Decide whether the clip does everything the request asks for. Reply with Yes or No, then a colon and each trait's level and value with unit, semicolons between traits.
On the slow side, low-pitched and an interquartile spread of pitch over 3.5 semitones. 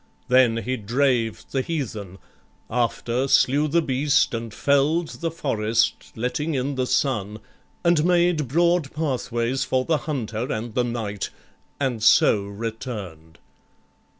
Yes: slow, 125 wpm; low, 130 Hz; average, 4.4 semitones